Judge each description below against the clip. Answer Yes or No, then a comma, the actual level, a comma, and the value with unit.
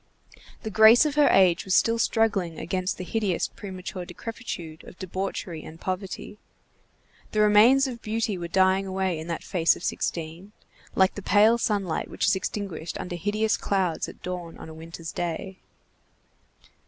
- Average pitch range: Yes, average, 3.6 semitones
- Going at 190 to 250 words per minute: No, average, 160 wpm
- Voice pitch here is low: No, high, 190 Hz